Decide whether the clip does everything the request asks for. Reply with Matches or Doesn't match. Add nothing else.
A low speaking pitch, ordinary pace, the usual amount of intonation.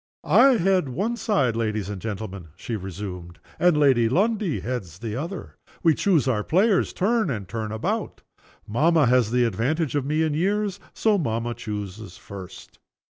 Doesn't match